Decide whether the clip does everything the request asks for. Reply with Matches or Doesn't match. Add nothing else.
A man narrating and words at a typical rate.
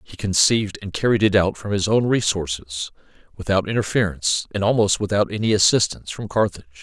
Matches